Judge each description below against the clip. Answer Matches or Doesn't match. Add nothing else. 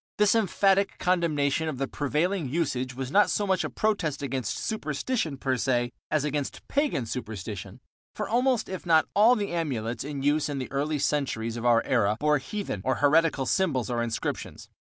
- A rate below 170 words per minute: Doesn't match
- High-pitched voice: Doesn't match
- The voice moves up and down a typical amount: Doesn't match